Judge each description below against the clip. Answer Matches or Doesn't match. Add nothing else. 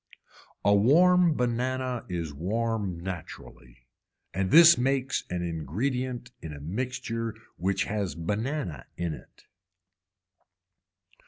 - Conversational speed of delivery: Doesn't match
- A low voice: Matches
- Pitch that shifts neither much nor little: Doesn't match